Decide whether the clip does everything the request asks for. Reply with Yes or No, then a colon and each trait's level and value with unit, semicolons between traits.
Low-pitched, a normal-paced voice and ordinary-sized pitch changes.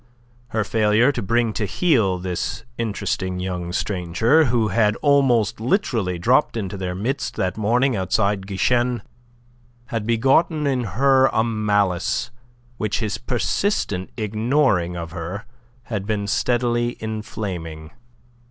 No: low, 110 Hz; slow, 125 wpm; average, 4.3 semitones